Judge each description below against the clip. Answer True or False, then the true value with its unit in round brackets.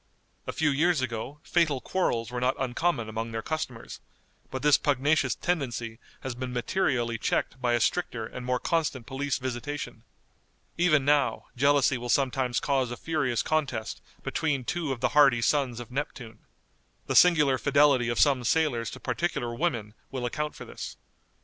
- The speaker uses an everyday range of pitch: True (3.5 semitones)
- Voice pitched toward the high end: False (130 Hz)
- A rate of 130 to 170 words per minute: True (160 wpm)